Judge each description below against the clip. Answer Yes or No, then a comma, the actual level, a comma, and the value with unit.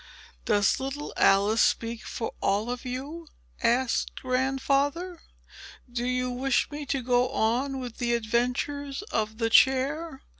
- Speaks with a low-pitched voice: No, very high, 255 Hz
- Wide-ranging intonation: No, average, 2.7 semitones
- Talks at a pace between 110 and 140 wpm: Yes, slow, 135 wpm